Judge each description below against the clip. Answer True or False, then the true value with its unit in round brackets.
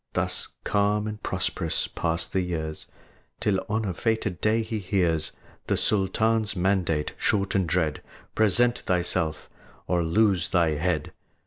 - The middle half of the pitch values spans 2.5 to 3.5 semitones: False (4.0 semitones)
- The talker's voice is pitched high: False (95 Hz)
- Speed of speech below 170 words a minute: True (135 wpm)